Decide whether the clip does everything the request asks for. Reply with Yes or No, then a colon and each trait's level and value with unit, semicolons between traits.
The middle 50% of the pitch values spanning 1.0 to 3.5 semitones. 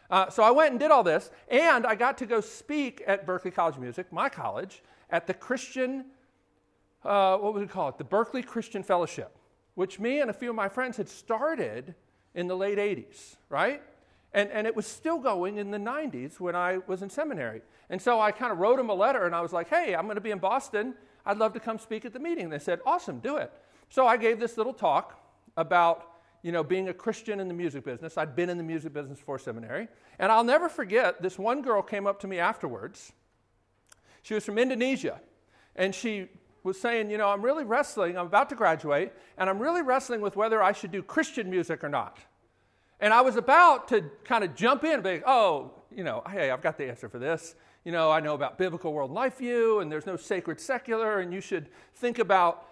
No: wide, 5.5 semitones